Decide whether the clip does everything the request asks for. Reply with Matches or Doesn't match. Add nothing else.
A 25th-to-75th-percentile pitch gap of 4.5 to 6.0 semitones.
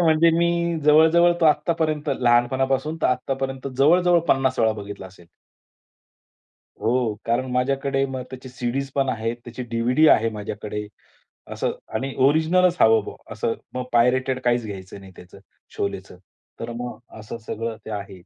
Matches